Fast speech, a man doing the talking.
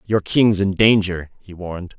No: average, 180 wpm; male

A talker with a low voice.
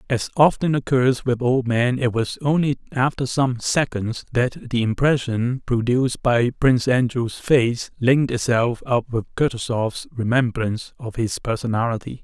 Yes: low, 125 Hz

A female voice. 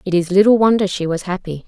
Yes: female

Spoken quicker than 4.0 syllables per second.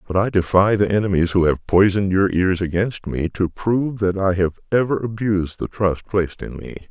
Yes: 5.4 syllables/s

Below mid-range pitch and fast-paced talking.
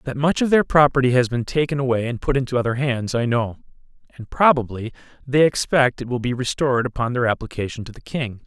Yes: low, 125 Hz; fast, 215 wpm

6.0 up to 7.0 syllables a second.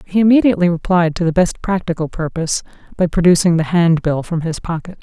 Yes: 6.1 syllables/s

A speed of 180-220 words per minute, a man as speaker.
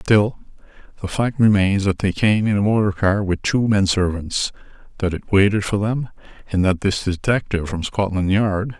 Yes: average, 185 wpm; male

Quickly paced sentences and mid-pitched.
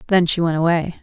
Yes: fast, 235 wpm; medium, 170 Hz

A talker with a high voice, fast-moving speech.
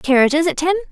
No: very high, 305 Hz; average, 195 wpm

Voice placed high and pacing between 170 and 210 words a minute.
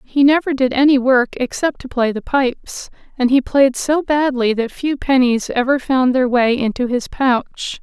Yes: very high, 260 Hz; average, 190 wpm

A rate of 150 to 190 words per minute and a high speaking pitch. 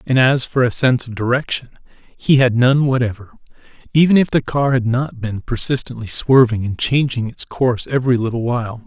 No: average, 175 wpm; low, 125 Hz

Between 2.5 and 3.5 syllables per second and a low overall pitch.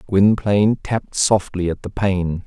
No: 4.4 syllables/s; low, 100 Hz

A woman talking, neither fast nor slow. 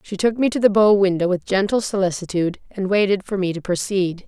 No: female; fast, 225 wpm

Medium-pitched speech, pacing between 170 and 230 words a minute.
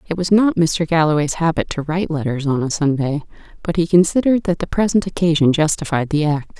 Yes: medium, 165 Hz; average, 200 wpm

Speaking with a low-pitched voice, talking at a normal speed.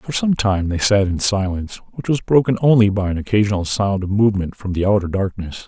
No: low, 100 Hz; fast, 220 wpm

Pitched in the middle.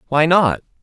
Yes: medium, 155 Hz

